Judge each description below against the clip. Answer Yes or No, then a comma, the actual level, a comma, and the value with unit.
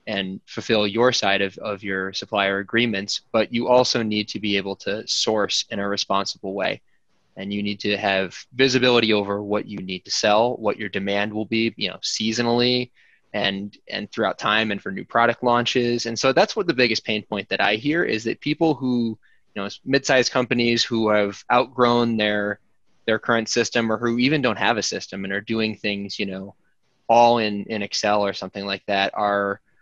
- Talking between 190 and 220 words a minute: Yes, average, 200 wpm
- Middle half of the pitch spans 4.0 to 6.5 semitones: No, average, 2.9 semitones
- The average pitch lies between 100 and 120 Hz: Yes, low, 110 Hz